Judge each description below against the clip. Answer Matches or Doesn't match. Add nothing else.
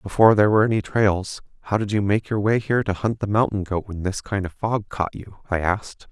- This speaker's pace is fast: Matches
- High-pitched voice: Doesn't match